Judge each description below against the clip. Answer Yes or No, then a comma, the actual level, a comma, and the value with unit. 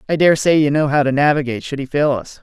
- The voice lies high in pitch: No, medium, 145 Hz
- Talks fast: Yes, fast, 295 wpm